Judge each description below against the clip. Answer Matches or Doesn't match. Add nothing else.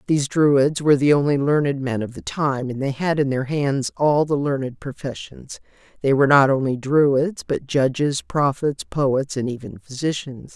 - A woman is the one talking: Matches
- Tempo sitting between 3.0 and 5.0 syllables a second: Matches